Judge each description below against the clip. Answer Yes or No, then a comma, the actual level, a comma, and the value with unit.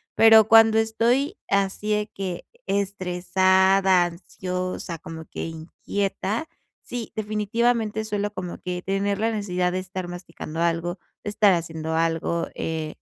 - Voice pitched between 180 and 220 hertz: Yes, high, 190 Hz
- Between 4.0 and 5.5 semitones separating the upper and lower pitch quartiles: No, average, 3.2 semitones